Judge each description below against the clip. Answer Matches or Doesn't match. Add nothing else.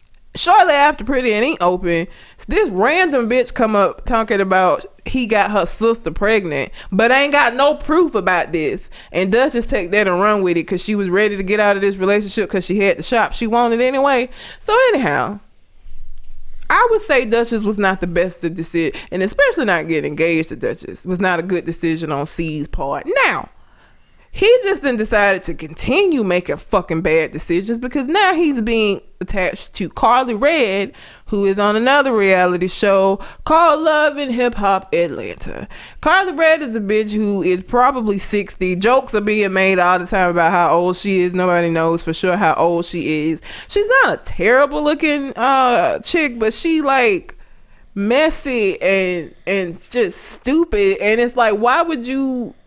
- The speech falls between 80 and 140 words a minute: Doesn't match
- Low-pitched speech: Doesn't match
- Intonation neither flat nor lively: Doesn't match